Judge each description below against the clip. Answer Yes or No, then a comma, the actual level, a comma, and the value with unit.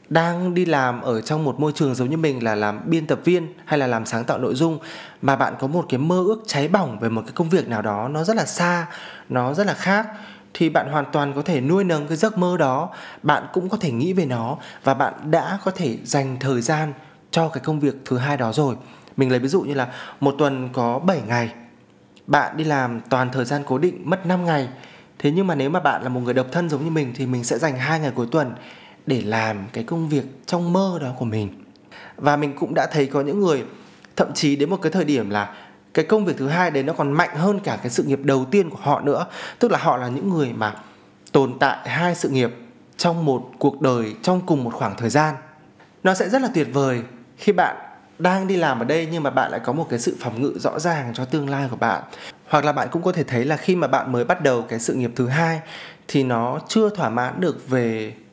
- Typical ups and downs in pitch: Yes, average, 4.9 semitones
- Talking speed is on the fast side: Yes, fast, 255 wpm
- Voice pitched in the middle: Yes, medium, 145 Hz